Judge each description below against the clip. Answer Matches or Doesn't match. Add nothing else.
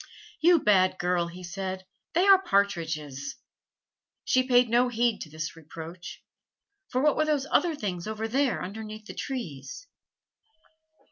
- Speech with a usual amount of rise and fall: Doesn't match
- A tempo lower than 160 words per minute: Matches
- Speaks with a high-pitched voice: Matches